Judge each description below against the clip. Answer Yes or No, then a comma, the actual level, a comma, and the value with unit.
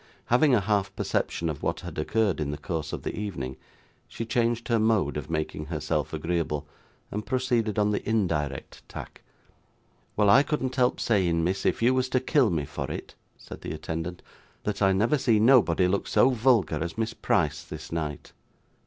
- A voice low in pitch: Yes, low, 100 Hz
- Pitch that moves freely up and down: Yes, wide, 6.2 semitones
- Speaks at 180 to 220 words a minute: Yes, average, 185 wpm